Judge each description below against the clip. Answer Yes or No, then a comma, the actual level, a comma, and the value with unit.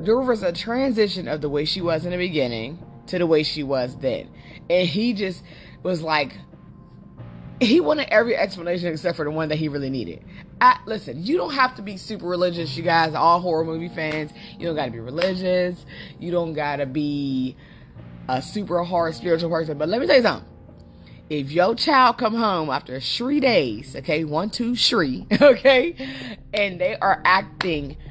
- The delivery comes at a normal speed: Yes, average, 185 wpm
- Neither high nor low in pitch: Yes, medium, 170 Hz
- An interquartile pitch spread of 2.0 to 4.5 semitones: No, average, 5.3 semitones